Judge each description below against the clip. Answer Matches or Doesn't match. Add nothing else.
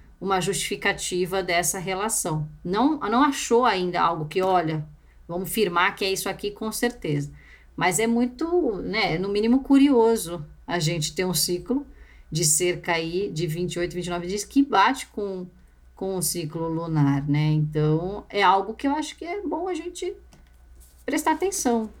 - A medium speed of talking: Matches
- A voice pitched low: Doesn't match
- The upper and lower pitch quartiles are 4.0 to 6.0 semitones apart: Matches